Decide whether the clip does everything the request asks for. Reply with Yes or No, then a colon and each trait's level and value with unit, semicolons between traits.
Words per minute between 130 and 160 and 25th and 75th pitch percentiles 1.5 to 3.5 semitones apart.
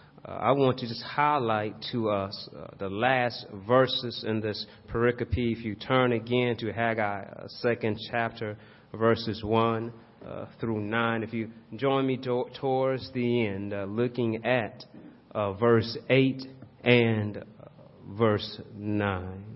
Yes: average, 140 wpm; average, 2.7 semitones